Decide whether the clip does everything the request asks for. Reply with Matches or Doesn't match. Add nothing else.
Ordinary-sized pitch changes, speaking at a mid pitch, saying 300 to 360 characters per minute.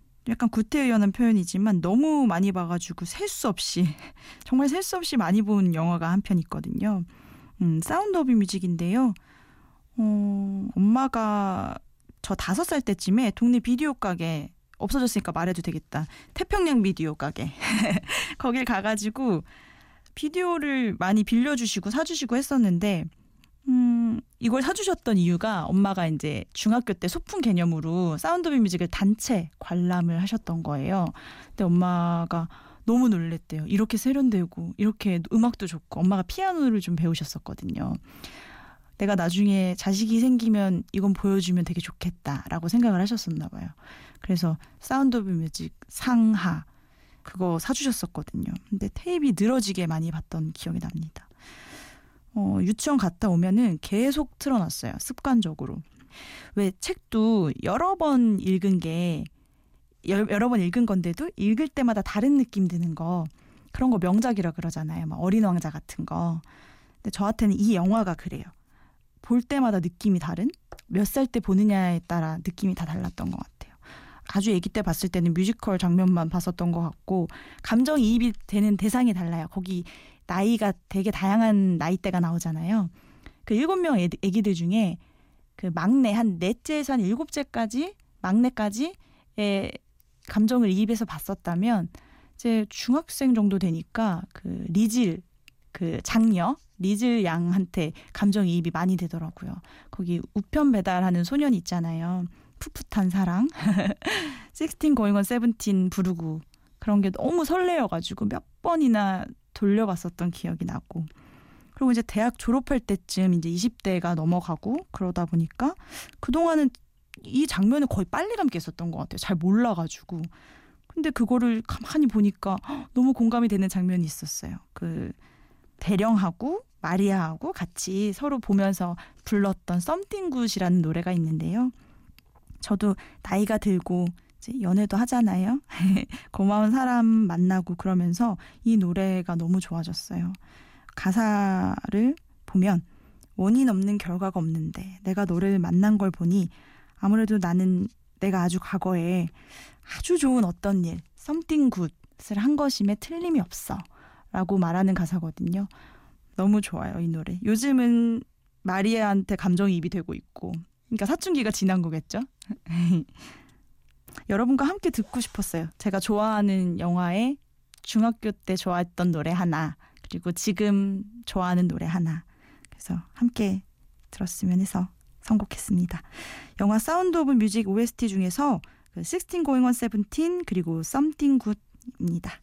Doesn't match